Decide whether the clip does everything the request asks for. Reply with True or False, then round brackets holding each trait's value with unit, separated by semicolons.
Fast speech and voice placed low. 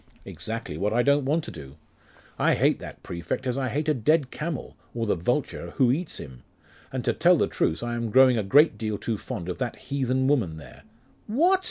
True (220 wpm; 120 Hz)